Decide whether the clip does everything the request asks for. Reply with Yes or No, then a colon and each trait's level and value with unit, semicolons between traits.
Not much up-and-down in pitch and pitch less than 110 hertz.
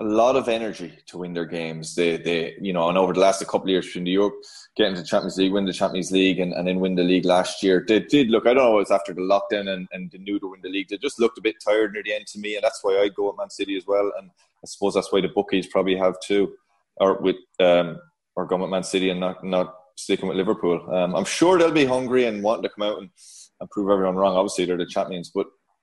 Yes: narrow, 1.9 semitones; very low, 95 Hz